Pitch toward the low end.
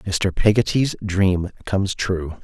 Yes: low, 100 Hz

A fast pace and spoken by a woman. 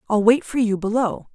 Yes: fast, 225 wpm; female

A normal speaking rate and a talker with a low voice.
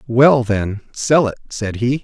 Yes: average, 175 wpm; low, 120 Hz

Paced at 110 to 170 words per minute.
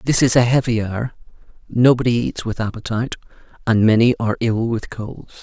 Yes: average, 165 wpm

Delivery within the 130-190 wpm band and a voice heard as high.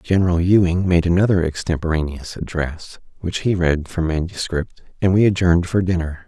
No: average, 155 wpm; very low, 85 Hz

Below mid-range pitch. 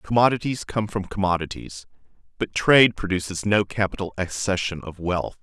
Yes: very low, 95 Hz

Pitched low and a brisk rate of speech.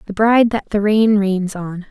No: high, 205 Hz; fast, 220 wpm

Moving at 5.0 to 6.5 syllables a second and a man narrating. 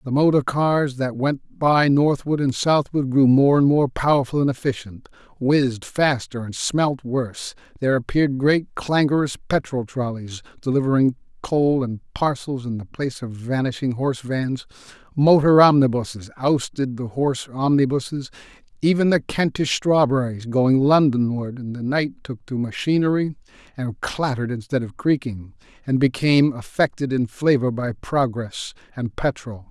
No: 4.7 syllables/s; male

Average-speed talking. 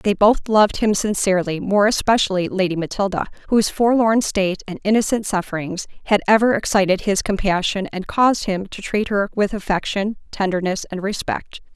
Yes: average, 160 wpm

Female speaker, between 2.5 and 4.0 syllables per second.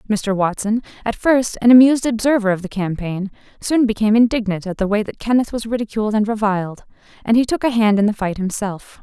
No: female; 6.1 syllables/s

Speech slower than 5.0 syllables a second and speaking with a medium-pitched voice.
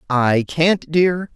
Yes: 2.7 syllables/s; medium, 155 Hz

